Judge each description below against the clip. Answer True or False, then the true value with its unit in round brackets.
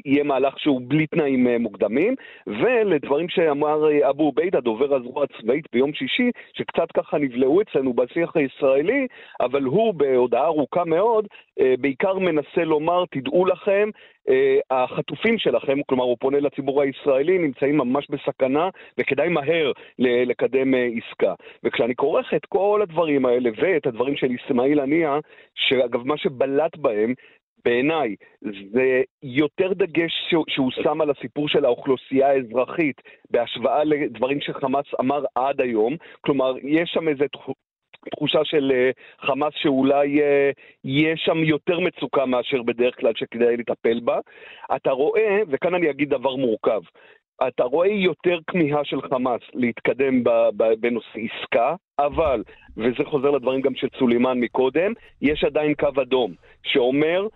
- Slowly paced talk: False (130 wpm)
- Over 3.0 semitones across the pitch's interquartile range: True (5.1 semitones)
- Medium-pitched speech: True (145 Hz)